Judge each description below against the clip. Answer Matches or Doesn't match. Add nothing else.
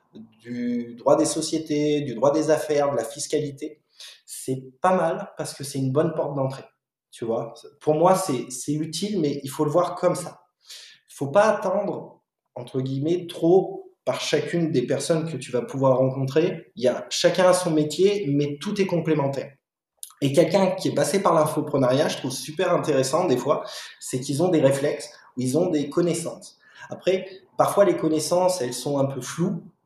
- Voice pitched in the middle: Matches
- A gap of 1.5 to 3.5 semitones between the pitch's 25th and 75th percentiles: Doesn't match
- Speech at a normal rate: Matches